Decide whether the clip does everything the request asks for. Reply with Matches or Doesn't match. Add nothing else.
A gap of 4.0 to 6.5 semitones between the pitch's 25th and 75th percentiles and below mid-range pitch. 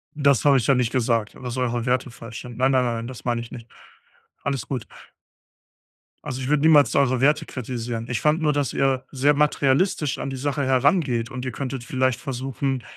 Doesn't match